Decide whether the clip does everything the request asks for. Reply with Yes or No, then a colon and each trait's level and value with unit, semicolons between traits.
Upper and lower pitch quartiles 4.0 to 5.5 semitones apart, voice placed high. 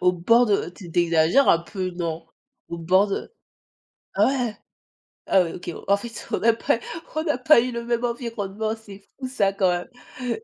Yes: average, 5.0 semitones; high, 205 Hz